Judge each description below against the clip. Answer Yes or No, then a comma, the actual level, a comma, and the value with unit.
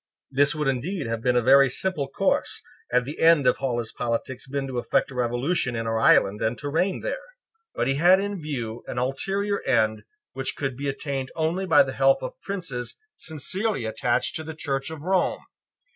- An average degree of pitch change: Yes, average, 5.0 semitones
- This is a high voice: No, low, 135 Hz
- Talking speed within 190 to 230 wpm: Yes, average, 200 wpm